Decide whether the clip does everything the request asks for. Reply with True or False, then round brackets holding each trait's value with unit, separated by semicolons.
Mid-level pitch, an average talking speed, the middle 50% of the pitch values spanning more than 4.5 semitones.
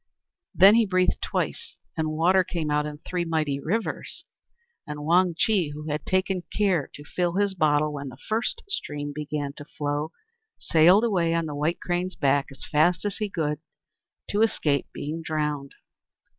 False (160 Hz; 170 wpm; 3.9 semitones)